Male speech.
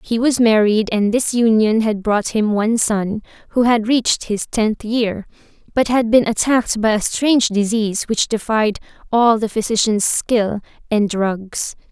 No: female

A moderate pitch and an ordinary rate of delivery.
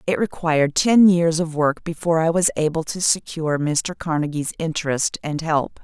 Yes: medium, 160 Hz; average, 175 wpm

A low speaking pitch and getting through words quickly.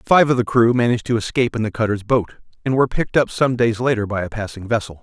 Yes: low, 115 Hz; fast, 265 wpm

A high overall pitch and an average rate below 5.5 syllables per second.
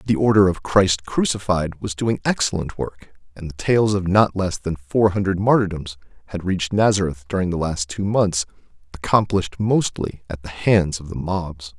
No: very low, 95 Hz; 4.8 syllables/s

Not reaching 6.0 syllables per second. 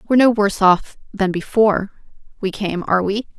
No: 6.1 syllables/s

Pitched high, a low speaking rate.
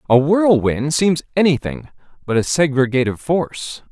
No: medium, 145 Hz; slow, 125 wpm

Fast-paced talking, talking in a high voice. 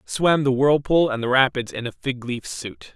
No: fast, 225 wpm; low, 130 Hz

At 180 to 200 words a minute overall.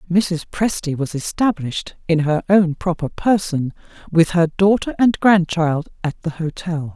No: average, 145 wpm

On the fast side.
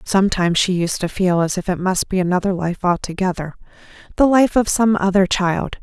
No: average, 195 wpm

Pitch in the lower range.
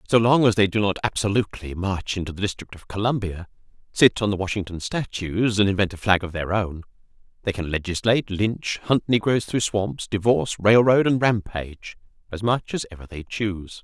Yes: low, 100 Hz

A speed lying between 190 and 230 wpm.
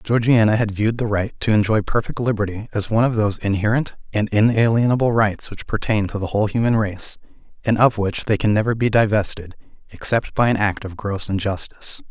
Yes: average, 195 wpm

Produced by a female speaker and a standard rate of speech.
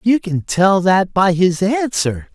No: male; average, 180 wpm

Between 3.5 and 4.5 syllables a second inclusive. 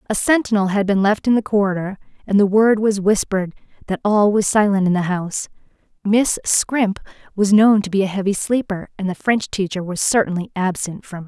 No: 5.6 syllables/s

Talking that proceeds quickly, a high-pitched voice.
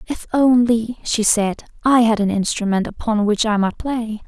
No: average, 180 wpm; high, 225 Hz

